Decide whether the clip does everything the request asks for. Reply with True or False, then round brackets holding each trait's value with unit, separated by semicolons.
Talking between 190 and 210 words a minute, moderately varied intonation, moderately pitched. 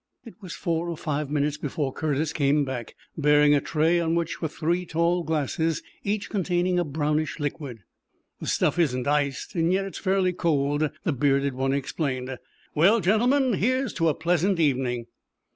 False (165 wpm; 3.7 semitones; 155 Hz)